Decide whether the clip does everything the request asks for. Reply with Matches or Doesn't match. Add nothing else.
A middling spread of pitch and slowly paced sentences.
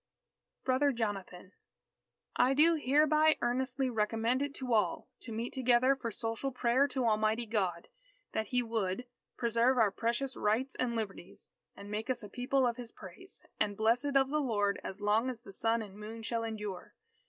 Doesn't match